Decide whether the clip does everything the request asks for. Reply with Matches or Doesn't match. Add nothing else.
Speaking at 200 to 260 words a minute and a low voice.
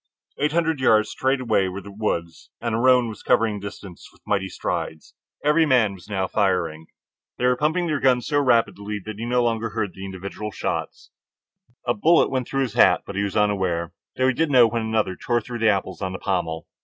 Matches